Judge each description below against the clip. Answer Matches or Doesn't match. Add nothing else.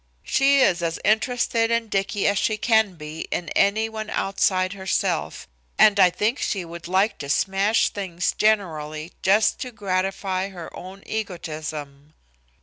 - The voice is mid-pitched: Doesn't match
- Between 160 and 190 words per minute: Doesn't match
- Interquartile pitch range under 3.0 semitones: Doesn't match